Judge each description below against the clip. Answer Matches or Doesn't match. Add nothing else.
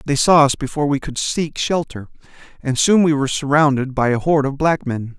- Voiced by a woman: Doesn't match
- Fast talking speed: Matches